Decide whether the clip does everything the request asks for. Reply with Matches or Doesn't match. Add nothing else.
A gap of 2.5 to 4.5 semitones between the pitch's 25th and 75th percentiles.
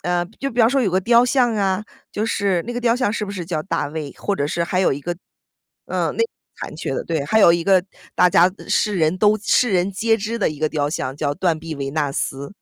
Doesn't match